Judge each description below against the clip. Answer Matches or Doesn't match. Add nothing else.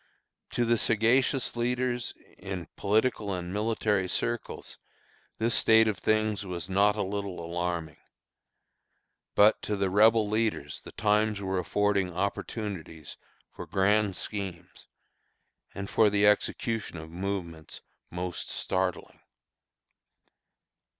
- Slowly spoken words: Matches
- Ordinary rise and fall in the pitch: Matches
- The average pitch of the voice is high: Doesn't match